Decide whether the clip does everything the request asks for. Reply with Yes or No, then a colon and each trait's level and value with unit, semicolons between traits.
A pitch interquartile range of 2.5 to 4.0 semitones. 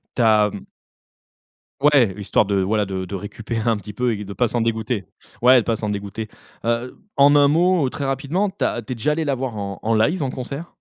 No: average, 4.7 semitones